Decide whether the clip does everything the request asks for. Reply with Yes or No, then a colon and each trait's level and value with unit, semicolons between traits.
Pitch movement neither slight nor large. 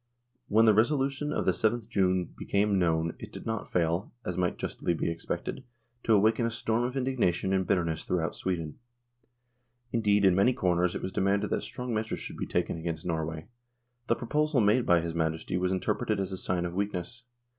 Yes: average, 4.4 semitones